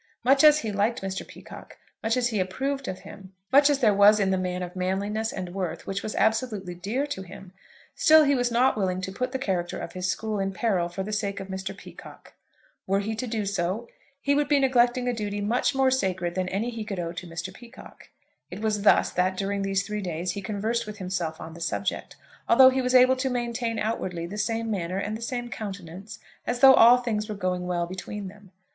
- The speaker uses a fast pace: Yes, fast, 230 wpm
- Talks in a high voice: Yes, high, 205 Hz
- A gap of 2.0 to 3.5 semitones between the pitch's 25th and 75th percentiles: No, average, 4.2 semitones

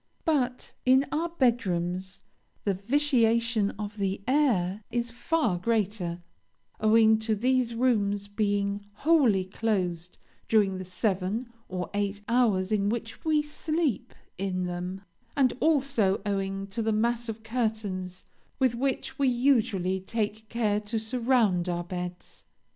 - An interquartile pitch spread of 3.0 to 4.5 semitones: Yes, average, 4.1 semitones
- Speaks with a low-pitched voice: No, high, 215 Hz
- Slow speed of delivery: Yes, slow, 130 wpm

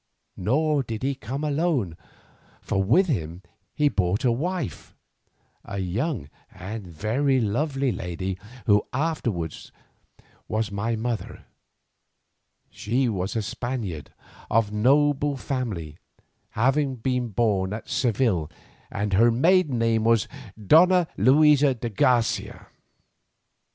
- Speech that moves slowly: Yes, slow, 110 wpm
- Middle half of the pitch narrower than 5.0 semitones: No, wide, 5.4 semitones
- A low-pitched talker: Yes, low, 115 Hz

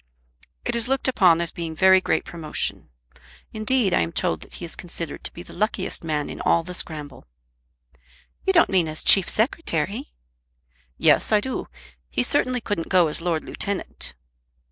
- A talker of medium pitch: Yes, medium, 175 Hz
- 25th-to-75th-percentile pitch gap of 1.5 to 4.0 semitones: No, average, 5.0 semitones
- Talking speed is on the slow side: No, average, 170 wpm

